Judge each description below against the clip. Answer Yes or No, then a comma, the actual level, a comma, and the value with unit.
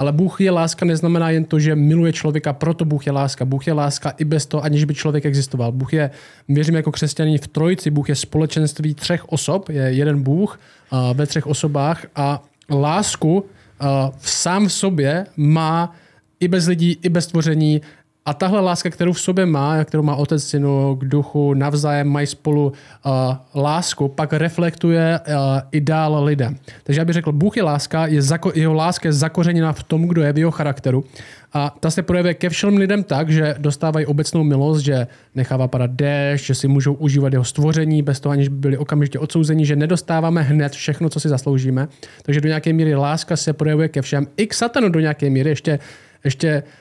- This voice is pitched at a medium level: Yes, medium, 150 Hz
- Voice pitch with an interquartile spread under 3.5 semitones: Yes, narrow, 2.4 semitones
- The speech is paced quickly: Yes, fast, 195 wpm